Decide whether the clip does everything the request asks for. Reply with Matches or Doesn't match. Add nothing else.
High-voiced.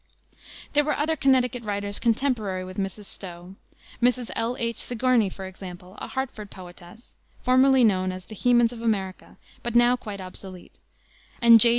Matches